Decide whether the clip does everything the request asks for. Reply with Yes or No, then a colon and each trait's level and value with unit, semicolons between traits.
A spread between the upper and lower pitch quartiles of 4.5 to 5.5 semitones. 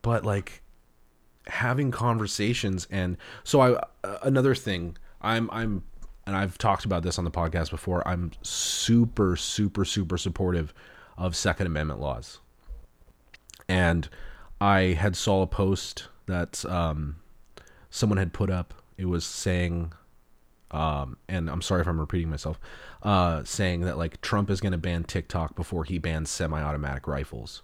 No: average, 3.2 semitones